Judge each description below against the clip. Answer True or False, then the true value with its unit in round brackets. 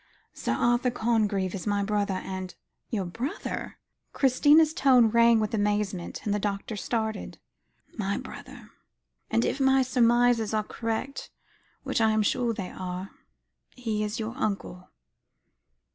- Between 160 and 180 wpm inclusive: False (140 wpm)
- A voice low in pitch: False (220 Hz)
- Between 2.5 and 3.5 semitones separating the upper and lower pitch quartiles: True (3.2 semitones)